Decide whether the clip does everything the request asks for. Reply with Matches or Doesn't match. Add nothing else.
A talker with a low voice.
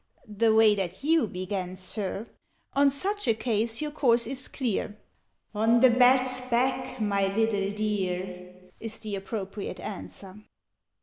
Doesn't match